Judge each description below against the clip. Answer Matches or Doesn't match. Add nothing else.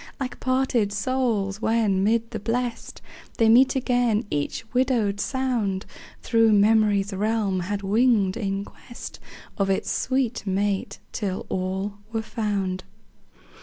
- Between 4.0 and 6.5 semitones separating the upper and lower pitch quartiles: Doesn't match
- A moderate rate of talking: Doesn't match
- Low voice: Doesn't match